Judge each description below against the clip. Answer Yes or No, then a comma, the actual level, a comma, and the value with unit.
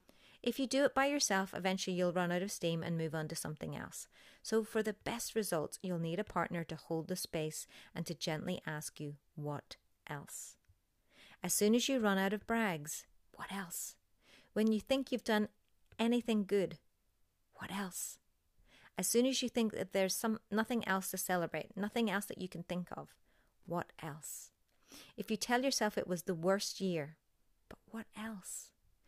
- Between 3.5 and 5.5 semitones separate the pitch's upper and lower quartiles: Yes, average, 4.9 semitones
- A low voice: No, high, 190 Hz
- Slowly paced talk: No, average, 185 wpm